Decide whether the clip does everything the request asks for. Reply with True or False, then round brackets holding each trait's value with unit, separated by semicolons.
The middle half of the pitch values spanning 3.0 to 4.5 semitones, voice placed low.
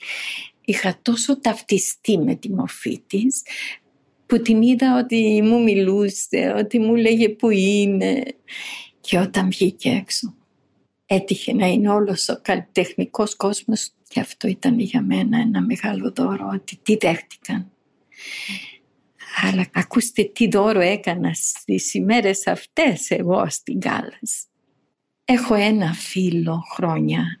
False (3.5 semitones; 215 Hz)